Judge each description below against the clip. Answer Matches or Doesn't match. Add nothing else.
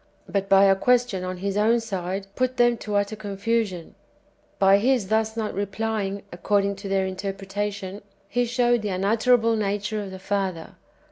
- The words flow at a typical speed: Matches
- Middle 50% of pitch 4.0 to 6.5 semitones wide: Doesn't match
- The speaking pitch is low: Doesn't match